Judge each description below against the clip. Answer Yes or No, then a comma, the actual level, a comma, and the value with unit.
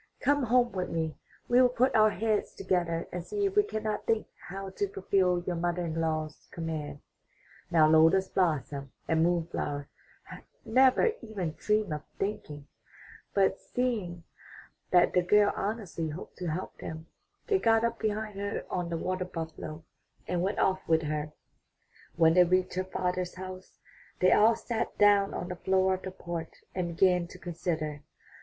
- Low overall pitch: No, medium, 185 Hz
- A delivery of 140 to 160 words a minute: No, average, 170 wpm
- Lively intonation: No, average, 4.2 semitones